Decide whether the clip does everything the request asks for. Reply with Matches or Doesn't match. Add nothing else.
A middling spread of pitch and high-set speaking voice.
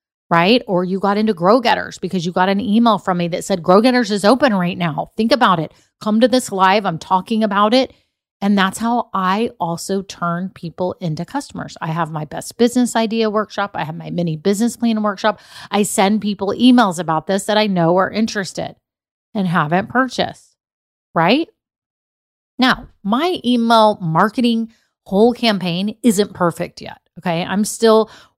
Matches